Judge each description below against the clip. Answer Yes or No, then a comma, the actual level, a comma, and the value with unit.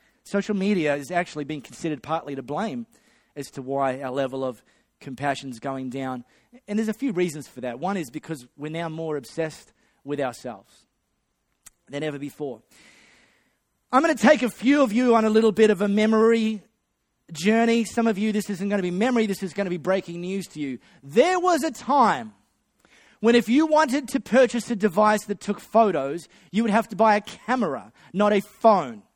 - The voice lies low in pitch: No, high, 200 Hz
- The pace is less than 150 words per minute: No, average, 200 wpm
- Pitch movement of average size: No, wide, 7.4 semitones